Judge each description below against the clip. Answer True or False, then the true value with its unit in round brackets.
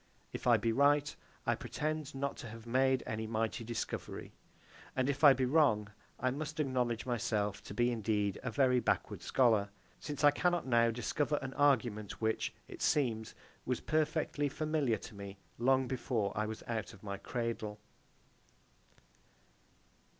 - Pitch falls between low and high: False (125 Hz)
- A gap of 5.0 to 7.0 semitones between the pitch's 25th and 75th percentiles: False (4.2 semitones)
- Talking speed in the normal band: True (155 wpm)